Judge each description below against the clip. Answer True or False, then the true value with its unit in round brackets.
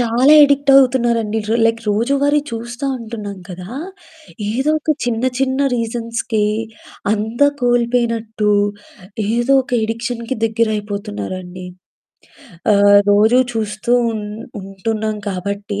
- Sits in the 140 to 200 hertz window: False (225 Hz)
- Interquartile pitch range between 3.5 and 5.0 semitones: False (2.7 semitones)